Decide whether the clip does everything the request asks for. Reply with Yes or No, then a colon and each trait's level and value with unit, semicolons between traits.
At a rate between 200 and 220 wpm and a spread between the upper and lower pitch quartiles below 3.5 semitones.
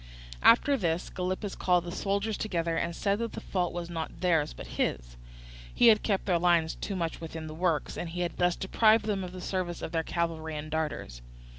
Yes: fast, 205 wpm; average, 3.0 semitones